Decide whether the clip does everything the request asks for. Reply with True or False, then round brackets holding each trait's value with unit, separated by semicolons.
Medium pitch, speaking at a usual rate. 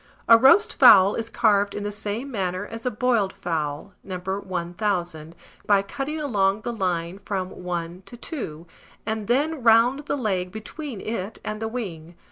False (205 Hz; 170 wpm)